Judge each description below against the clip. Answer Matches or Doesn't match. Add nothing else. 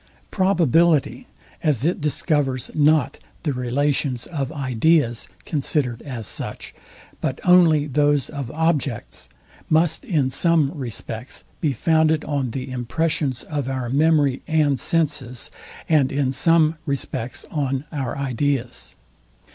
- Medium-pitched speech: Matches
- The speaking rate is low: Matches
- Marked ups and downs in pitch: Doesn't match